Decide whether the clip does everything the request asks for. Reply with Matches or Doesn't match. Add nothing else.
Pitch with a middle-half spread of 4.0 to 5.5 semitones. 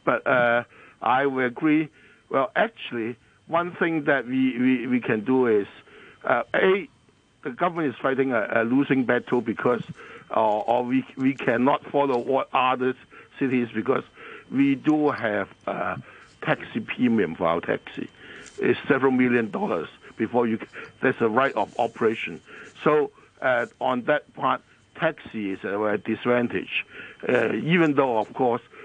Matches